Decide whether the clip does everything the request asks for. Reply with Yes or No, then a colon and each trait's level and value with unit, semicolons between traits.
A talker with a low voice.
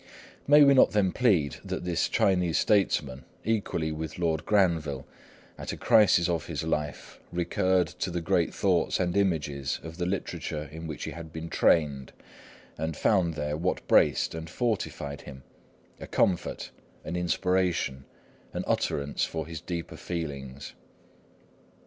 Yes: very low, 85 Hz